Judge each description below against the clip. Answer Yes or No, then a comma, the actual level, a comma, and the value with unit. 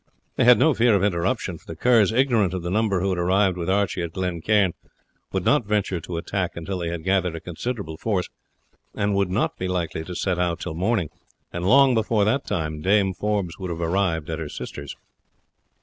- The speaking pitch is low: Yes, very low, 95 Hz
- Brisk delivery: Yes, fast, 210 wpm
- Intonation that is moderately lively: Yes, average, 3.5 semitones